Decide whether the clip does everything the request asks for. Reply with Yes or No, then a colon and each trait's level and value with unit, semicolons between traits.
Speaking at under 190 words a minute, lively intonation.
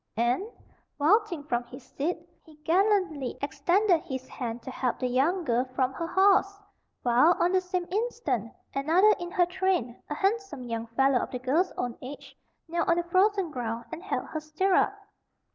Yes: average, 175 wpm; wide, 6.5 semitones